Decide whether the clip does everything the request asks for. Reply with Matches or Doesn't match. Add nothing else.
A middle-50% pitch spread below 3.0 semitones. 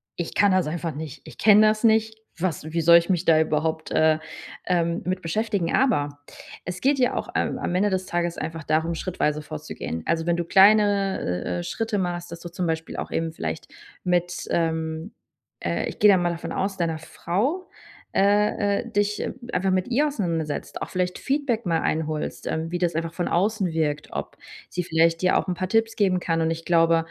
Doesn't match